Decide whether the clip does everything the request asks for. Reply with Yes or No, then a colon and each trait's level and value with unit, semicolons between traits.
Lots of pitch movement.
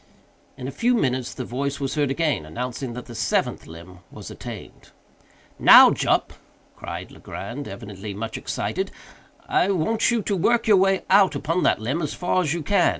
Yes: wide, 7.8 semitones